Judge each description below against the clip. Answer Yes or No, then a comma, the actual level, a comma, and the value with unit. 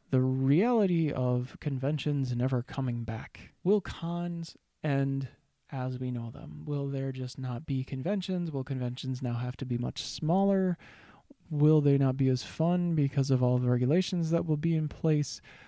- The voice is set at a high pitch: No, medium, 140 Hz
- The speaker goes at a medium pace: Yes, average, 170 wpm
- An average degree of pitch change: Yes, average, 4.2 semitones